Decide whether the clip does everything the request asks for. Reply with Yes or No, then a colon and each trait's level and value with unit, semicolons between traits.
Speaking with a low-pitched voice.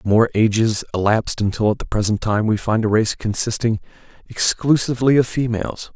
Yes: low, 110 Hz